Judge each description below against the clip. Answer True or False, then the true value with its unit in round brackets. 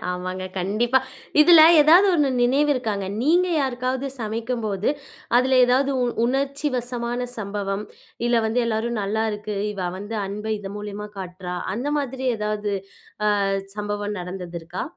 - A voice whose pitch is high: True (220 Hz)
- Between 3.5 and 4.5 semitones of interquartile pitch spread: True (4.1 semitones)